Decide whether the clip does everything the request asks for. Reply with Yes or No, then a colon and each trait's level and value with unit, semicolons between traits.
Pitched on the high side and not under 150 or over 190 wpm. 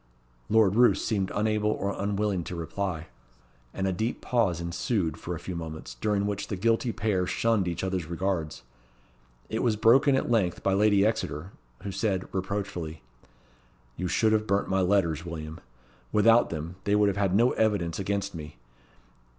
No: low, 100 Hz; average, 165 wpm